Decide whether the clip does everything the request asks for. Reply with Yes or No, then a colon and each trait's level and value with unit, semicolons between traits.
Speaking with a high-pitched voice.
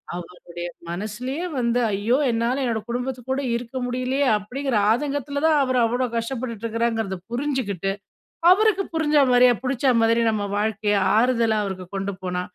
Yes: high, 235 Hz